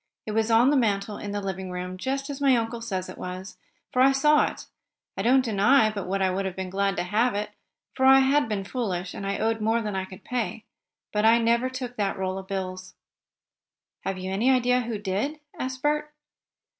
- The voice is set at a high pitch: Yes, high, 215 Hz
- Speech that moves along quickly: Yes, fast, 220 wpm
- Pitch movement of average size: Yes, average, 4.7 semitones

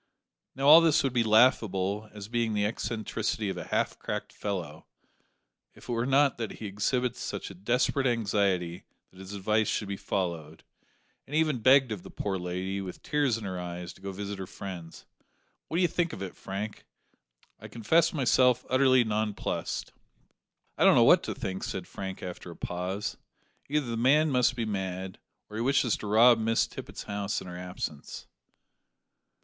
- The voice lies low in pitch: Yes, low, 105 Hz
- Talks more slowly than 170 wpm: No, average, 180 wpm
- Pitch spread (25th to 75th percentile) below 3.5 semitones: No, average, 4.7 semitones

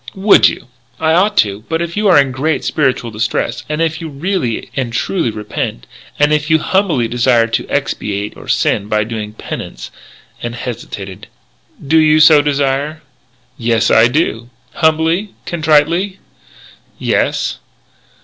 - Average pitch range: No, wide, 5.7 semitones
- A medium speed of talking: Yes, average, 150 wpm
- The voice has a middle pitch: Yes, medium, 145 Hz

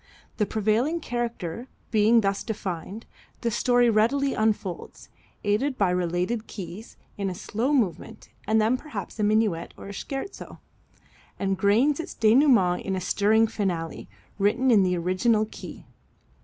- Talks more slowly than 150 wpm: Yes, slow, 135 wpm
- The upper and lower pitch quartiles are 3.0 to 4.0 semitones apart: Yes, average, 3.7 semitones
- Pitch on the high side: Yes, high, 215 Hz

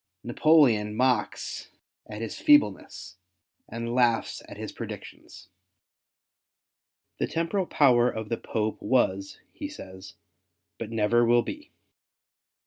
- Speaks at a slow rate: Yes, slow, 110 wpm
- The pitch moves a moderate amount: Yes, average, 4.0 semitones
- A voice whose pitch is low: Yes, low, 120 Hz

